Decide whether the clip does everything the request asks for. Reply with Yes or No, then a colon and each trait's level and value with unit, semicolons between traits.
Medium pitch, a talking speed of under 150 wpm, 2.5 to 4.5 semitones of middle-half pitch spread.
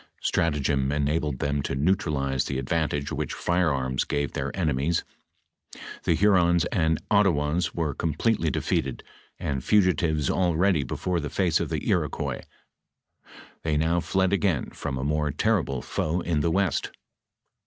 No: very low, 80 Hz; slow, 135 wpm; average, 3.8 semitones